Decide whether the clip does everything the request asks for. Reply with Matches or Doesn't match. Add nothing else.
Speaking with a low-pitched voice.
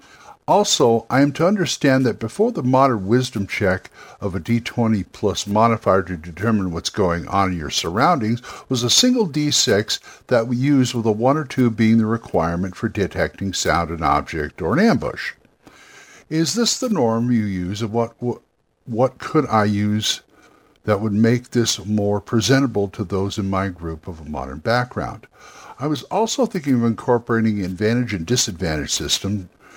Matches